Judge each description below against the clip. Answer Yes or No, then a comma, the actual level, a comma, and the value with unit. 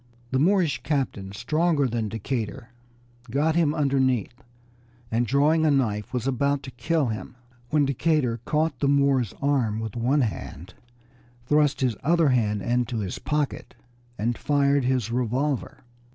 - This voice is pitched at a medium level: No, low, 130 Hz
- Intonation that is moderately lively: Yes, average, 3.9 semitones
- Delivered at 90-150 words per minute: Yes, average, 140 wpm